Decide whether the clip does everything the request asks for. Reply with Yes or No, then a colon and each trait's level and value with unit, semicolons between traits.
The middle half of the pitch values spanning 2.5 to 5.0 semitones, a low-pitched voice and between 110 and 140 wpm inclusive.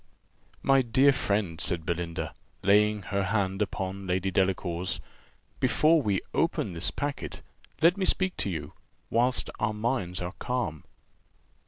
No: wide, 5.4 semitones; low, 100 Hz; slow, 135 wpm